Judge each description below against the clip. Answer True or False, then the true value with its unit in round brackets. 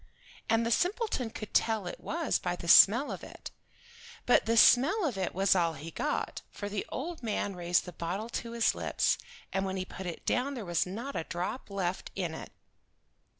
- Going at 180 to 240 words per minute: True (200 wpm)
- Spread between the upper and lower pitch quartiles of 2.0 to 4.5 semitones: False (5.3 semitones)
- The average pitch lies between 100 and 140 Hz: False (205 Hz)